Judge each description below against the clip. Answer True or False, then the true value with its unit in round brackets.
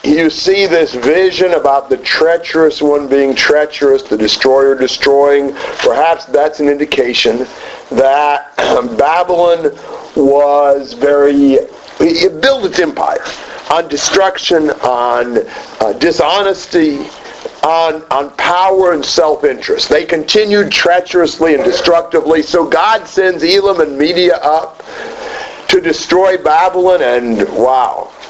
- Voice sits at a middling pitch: True (165 Hz)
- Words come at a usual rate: False (110 wpm)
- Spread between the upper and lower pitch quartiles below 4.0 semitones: False (4.9 semitones)